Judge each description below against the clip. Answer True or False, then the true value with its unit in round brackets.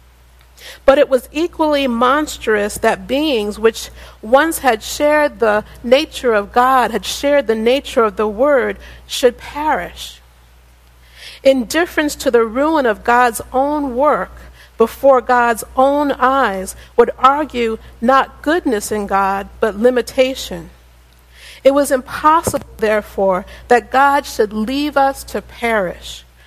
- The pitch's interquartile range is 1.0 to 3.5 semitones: False (4.9 semitones)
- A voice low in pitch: False (245 Hz)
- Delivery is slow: True (125 wpm)